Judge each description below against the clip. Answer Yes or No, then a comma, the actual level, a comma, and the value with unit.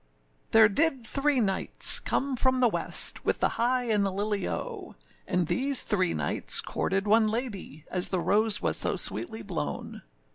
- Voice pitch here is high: Yes, high, 215 Hz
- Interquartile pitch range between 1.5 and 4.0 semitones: No, average, 4.6 semitones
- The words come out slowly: No, average, 175 wpm